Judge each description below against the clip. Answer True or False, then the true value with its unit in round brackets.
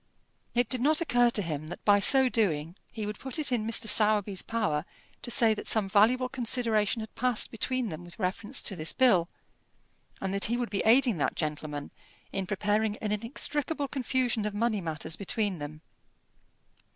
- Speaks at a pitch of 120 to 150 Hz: False (215 Hz)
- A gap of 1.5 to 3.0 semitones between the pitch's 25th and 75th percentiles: False (4.2 semitones)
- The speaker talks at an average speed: True (180 wpm)